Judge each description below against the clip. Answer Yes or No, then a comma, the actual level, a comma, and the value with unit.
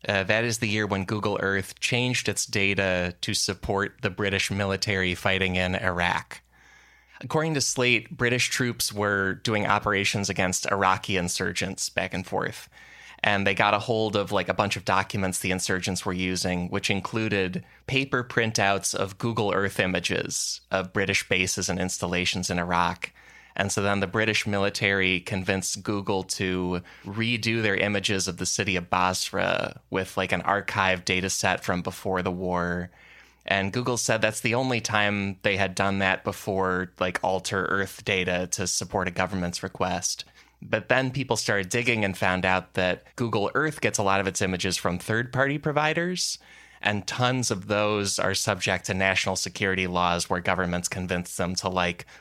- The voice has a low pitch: Yes, low, 100 Hz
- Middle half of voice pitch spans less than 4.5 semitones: Yes, average, 2.7 semitones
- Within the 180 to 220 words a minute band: No, average, 170 wpm